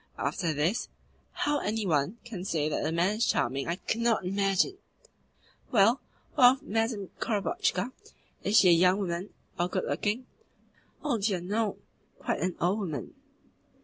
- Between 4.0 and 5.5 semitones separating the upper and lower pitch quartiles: Yes, average, 4.4 semitones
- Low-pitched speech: No, high, 200 Hz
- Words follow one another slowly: No, average, 150 wpm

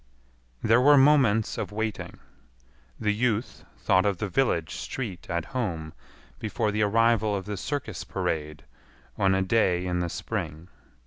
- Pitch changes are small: No, average, 4.2 semitones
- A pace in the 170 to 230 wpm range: No, average, 145 wpm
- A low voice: Yes, low, 105 Hz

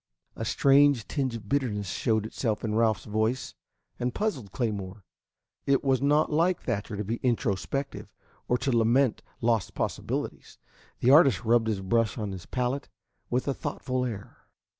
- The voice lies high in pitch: No, low, 120 Hz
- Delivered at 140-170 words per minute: Yes, average, 155 wpm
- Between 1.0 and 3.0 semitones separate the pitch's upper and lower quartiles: No, average, 4.1 semitones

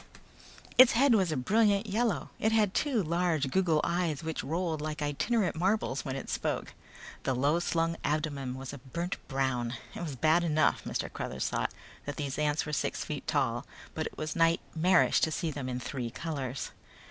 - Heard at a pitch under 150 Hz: No, medium, 155 Hz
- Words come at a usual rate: Yes, average, 180 wpm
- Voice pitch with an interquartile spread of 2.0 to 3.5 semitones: No, average, 4.4 semitones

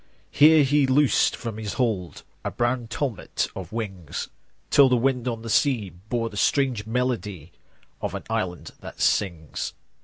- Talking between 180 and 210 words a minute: No, average, 160 wpm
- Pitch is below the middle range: Yes, low, 115 Hz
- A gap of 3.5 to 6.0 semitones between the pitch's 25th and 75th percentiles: Yes, average, 4.6 semitones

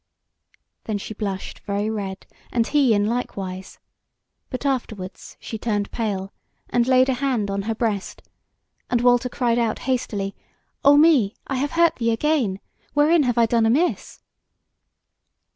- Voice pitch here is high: Yes, high, 230 Hz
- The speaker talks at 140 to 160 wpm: Yes, average, 150 wpm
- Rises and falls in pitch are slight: No, average, 4.1 semitones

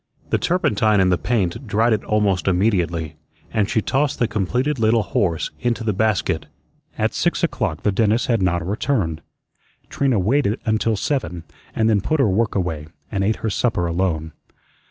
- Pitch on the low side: Yes, low, 105 Hz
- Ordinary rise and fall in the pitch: Yes, average, 3.9 semitones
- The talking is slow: No, average, 170 wpm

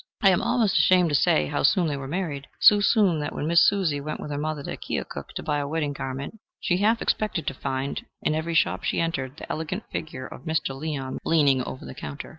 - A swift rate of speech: Yes, fast, 235 wpm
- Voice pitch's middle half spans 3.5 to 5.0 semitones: Yes, average, 3.9 semitones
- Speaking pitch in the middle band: Yes, medium, 155 Hz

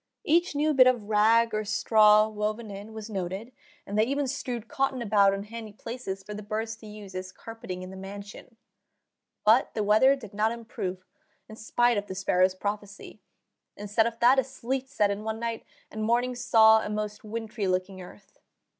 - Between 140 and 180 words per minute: No, average, 190 wpm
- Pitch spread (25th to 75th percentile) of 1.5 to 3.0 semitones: Yes, narrow, 2.5 semitones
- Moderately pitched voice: No, high, 215 Hz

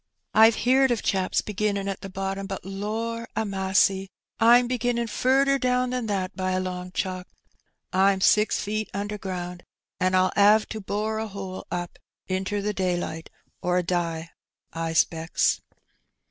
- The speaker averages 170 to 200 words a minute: No, average, 155 wpm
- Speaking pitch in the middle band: No, high, 195 Hz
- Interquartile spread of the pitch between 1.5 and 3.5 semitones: Yes, average, 2.9 semitones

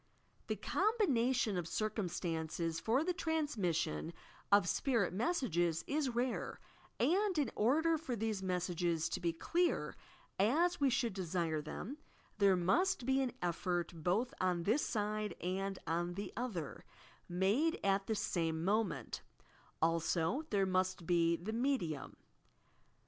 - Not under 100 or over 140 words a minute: Yes, slow, 135 wpm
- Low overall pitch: No, high, 200 Hz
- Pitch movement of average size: No, wide, 7.0 semitones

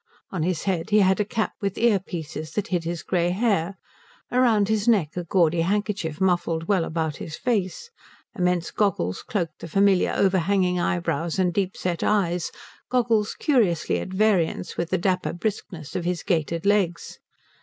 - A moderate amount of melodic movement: Yes, average, 3.3 semitones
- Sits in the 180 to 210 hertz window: Yes, medium, 185 Hz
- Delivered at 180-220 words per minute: No, average, 165 wpm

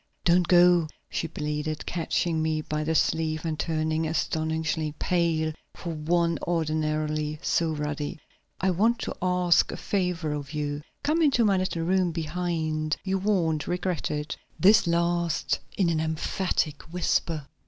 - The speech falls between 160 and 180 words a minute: No, average, 145 wpm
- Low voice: No, medium, 160 Hz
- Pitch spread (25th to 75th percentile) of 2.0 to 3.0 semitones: Yes, narrow, 2.4 semitones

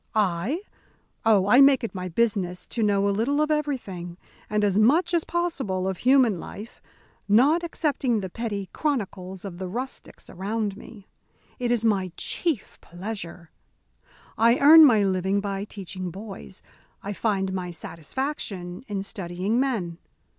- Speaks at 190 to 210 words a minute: No, average, 145 wpm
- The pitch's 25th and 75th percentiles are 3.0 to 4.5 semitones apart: No, average, 5.1 semitones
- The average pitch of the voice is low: No, high, 205 Hz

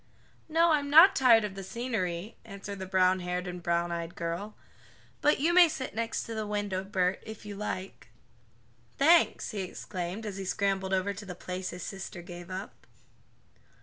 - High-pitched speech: Yes, high, 195 Hz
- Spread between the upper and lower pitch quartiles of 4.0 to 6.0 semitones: No, average, 3.6 semitones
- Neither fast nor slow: Yes, average, 165 wpm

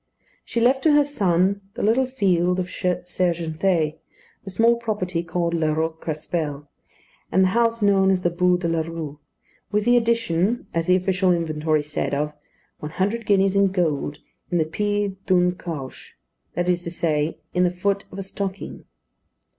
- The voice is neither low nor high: Yes, medium, 180 Hz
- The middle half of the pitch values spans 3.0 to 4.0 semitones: Yes, average, 3.4 semitones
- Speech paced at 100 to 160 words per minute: No, average, 170 wpm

